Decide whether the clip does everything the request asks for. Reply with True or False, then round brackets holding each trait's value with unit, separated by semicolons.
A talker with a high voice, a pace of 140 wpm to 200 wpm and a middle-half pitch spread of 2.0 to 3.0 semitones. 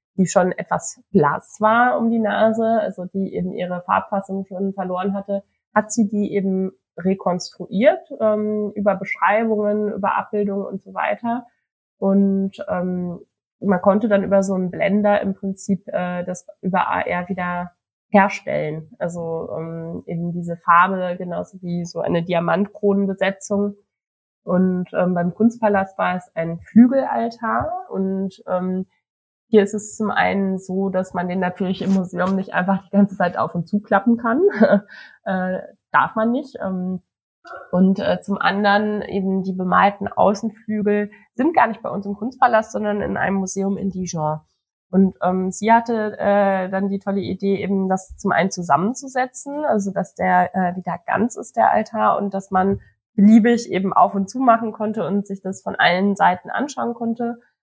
True (195 Hz; 160 wpm; 2.4 semitones)